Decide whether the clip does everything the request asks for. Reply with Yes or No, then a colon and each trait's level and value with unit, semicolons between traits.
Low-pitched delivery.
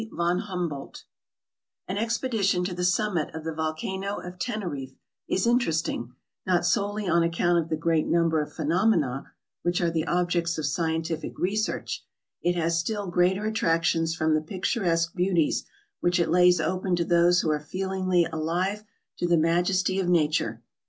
No: medium, 175 Hz